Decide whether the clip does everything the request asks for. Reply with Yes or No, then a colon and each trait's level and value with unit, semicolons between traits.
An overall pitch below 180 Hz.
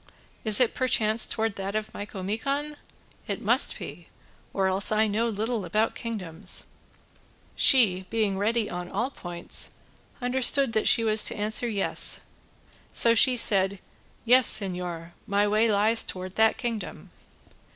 No: high, 215 Hz